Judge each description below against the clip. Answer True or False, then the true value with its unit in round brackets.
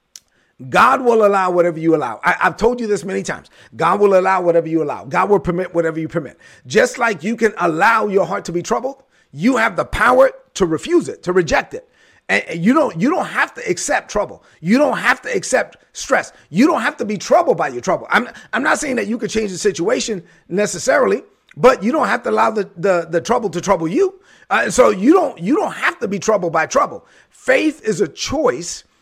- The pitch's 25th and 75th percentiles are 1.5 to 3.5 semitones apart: False (4.8 semitones)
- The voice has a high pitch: True (205 Hz)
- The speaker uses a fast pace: True (230 wpm)